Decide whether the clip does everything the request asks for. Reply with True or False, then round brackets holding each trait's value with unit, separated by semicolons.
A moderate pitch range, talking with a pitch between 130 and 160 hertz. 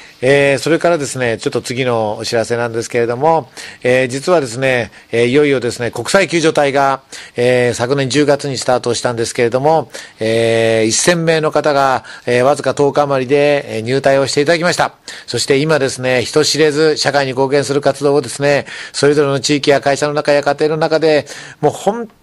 True (3.2 semitones; 140 Hz)